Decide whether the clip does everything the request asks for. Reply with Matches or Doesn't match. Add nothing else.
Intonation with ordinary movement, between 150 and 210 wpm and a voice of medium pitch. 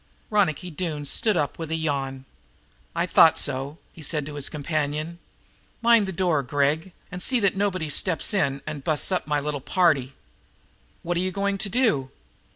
Matches